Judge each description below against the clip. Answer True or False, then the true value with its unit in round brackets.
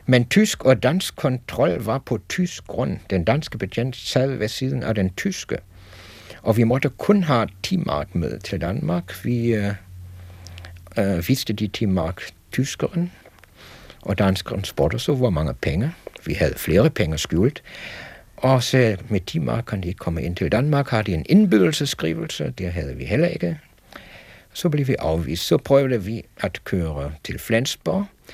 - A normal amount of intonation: False (6.4 semitones)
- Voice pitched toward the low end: True (110 Hz)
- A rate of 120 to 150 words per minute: False (160 wpm)